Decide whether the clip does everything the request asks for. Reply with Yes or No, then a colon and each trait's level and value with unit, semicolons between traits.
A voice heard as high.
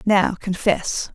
Yes: high, 195 Hz